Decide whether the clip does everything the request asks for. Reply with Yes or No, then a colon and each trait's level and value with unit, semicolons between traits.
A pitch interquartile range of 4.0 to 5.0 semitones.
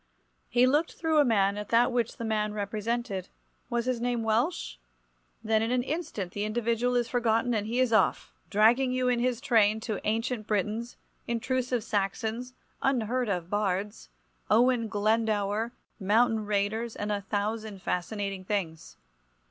No: average, 2.8 semitones